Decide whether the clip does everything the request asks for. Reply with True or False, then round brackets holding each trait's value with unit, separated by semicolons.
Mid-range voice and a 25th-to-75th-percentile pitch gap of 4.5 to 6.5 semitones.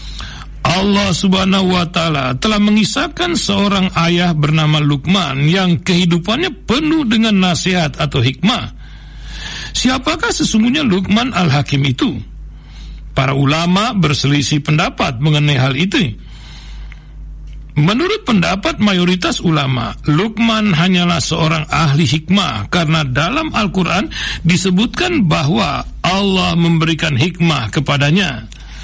True (175 Hz; 4.8 semitones)